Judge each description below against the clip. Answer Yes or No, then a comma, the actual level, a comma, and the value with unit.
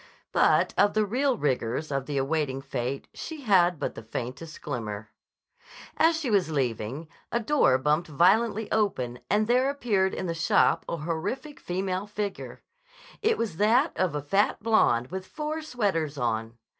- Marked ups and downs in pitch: Yes, wide, 8.2 semitones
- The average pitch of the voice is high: No, medium, 175 Hz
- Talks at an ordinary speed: Yes, average, 160 wpm